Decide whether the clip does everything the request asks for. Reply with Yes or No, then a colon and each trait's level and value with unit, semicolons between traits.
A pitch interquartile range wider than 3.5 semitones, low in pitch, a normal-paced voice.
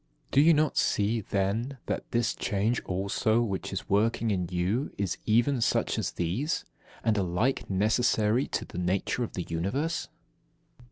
Yes: average, 3.9 semitones; low, 110 Hz; average, 155 wpm